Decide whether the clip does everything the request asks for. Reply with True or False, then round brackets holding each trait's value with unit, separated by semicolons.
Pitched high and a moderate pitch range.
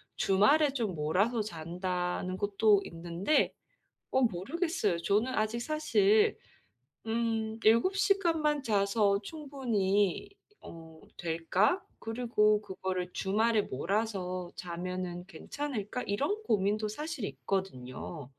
True (205 Hz; 4.6 semitones)